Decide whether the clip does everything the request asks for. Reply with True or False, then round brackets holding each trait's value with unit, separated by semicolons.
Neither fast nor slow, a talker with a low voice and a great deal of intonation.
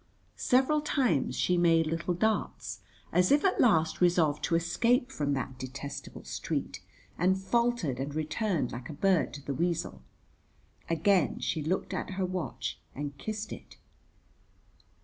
False (145 wpm; 175 Hz; 5.9 semitones)